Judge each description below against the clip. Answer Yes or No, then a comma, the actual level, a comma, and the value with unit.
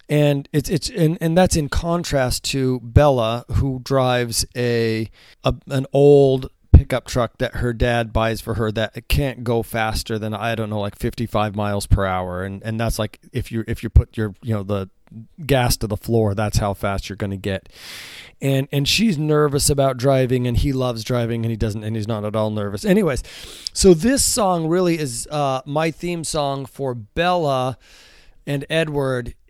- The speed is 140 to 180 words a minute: No, average, 190 wpm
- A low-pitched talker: Yes, low, 120 Hz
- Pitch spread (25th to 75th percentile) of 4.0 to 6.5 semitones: Yes, average, 4.3 semitones